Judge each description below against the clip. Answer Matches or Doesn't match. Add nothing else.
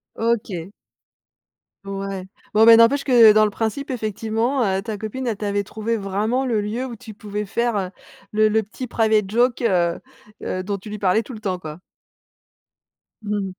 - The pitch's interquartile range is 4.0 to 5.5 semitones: Doesn't match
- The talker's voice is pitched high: Matches